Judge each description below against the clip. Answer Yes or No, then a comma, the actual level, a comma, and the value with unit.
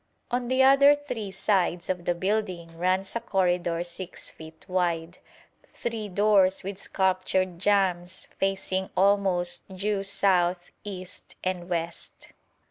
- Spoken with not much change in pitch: Yes, narrow, 2.3 semitones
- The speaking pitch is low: No, medium, 185 Hz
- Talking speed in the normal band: No, slow, 125 wpm